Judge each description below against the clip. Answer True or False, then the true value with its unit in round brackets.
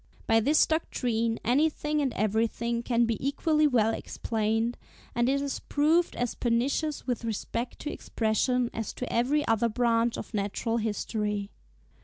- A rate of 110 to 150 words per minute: True (145 wpm)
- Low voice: False (235 Hz)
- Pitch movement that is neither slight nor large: True (3.7 semitones)